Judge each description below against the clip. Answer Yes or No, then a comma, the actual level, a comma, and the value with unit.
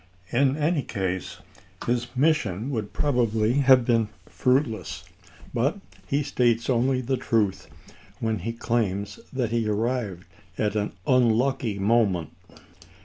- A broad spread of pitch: No, average, 3.4 semitones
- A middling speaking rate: No, slow, 120 wpm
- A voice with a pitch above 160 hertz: No, low, 115 Hz